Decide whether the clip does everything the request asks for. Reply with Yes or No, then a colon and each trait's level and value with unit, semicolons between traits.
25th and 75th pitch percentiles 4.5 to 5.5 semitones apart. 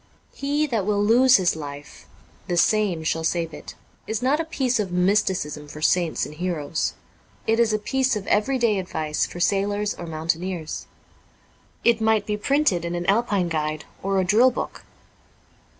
Yes: average, 4.9 semitones